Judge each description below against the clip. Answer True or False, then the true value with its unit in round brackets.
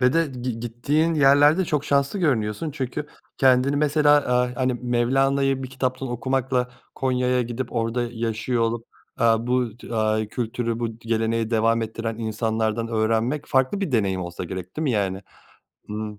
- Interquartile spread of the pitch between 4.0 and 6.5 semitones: False (2.9 semitones)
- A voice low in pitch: True (120 Hz)